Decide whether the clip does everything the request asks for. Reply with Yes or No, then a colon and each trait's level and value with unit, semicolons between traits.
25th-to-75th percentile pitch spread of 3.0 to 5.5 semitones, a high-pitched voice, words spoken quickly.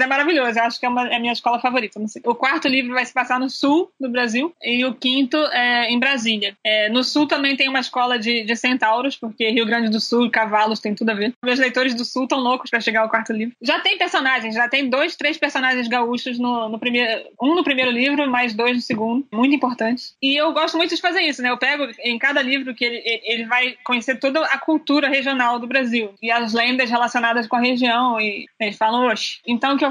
No: narrow, 2.6 semitones; very high, 250 Hz; fast, 245 wpm